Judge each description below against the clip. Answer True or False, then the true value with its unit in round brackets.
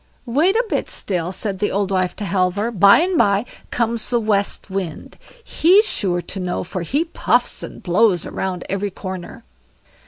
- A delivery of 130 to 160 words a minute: False (180 wpm)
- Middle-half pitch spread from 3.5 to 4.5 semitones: True (4.1 semitones)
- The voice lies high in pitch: True (200 Hz)